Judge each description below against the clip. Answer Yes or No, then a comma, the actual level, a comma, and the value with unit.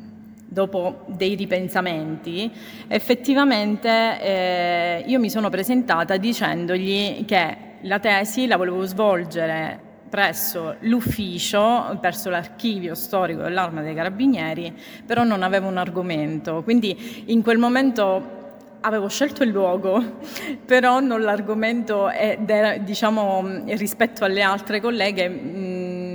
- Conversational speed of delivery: No, slow, 110 wpm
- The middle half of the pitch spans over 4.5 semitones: No, average, 3.8 semitones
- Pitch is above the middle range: Yes, high, 200 Hz